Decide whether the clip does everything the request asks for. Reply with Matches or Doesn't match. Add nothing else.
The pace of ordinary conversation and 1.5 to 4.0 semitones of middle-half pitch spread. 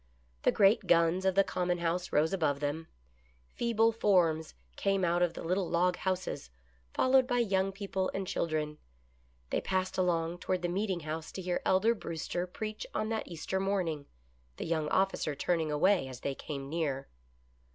Matches